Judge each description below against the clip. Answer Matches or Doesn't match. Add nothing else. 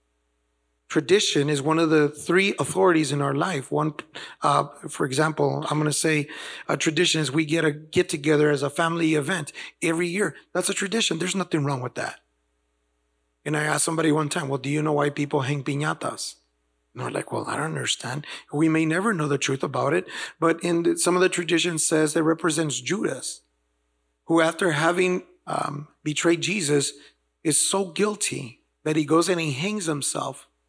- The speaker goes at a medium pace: Matches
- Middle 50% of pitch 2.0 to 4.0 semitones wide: Matches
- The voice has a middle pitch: Matches